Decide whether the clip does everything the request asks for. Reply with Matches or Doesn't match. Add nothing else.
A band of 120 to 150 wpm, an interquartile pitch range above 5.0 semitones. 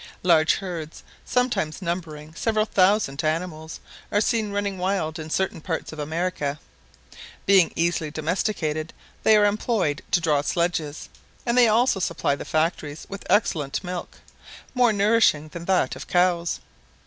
Doesn't match